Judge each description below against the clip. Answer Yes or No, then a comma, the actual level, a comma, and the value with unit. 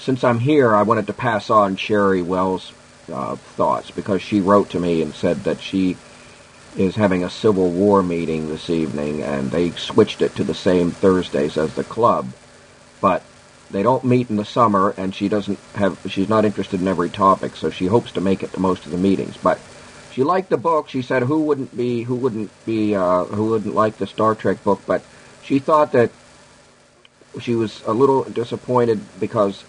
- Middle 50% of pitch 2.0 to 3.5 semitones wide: No, average, 4.1 semitones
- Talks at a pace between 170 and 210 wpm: Yes, average, 200 wpm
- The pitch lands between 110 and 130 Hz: No, low, 100 Hz